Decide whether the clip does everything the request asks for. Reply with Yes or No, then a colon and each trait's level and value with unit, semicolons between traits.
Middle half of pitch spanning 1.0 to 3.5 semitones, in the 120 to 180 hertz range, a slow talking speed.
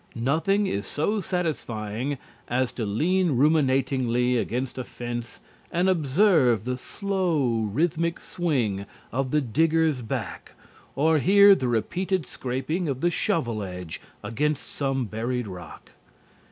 No: wide, 5.6 semitones; low, 135 Hz; slow, 125 wpm